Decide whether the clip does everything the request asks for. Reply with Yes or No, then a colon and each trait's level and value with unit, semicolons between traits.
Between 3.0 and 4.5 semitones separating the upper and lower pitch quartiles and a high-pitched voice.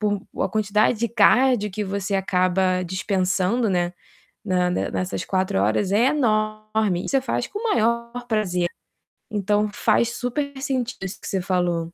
Yes: average, 4.0 semitones; high, 205 Hz